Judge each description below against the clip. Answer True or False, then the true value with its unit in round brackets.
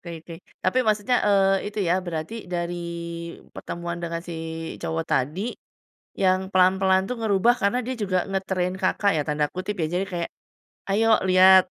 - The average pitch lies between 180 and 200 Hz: True (185 Hz)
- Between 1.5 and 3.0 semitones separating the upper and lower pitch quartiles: True (2.7 semitones)